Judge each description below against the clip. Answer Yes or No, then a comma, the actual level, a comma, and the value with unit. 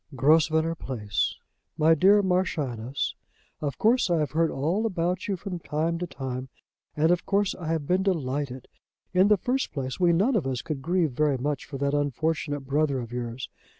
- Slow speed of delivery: No, average, 185 wpm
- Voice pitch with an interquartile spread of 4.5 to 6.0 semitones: Yes, average, 4.8 semitones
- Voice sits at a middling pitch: Yes, medium, 155 Hz